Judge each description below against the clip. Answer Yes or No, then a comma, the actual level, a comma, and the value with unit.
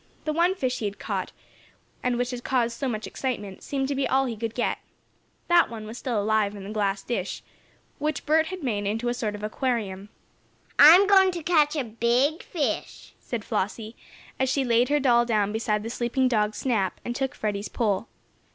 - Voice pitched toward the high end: Yes, high, 240 Hz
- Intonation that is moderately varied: Yes, average, 4.1 semitones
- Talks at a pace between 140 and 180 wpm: No, average, 200 wpm